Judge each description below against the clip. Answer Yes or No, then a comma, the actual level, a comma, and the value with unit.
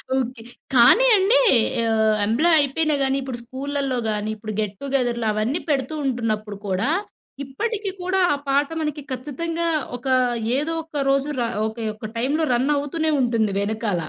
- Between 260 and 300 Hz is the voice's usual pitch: Yes, very high, 265 Hz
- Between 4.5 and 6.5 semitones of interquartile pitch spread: Yes, average, 5.0 semitones